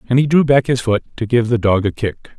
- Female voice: No, male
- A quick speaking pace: Yes, fast, 300 wpm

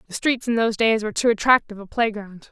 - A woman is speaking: Yes, female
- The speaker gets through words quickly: Yes, fast, 240 wpm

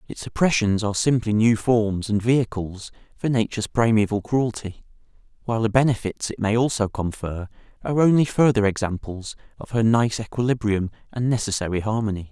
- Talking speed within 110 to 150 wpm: Yes, average, 145 wpm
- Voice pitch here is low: Yes, low, 110 Hz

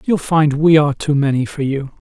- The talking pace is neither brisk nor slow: No, fast, 230 wpm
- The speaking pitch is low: No, medium, 145 Hz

